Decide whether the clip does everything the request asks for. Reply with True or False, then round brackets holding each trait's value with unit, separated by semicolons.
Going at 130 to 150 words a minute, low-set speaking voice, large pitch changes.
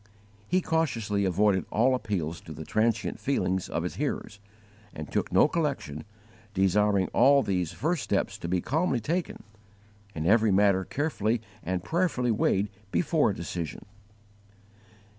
True (140 wpm; 105 Hz; 6.4 semitones)